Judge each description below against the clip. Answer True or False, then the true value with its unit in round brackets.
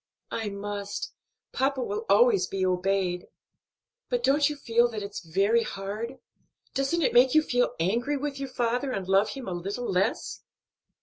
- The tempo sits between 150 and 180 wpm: True (165 wpm)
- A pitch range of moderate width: False (5.7 semitones)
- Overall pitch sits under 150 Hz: False (235 Hz)